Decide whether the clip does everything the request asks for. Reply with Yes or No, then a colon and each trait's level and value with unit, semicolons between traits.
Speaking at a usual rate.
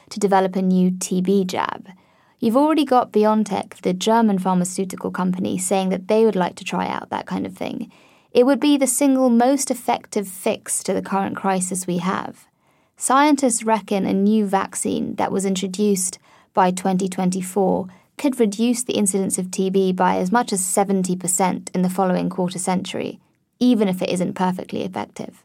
Yes: average, 170 wpm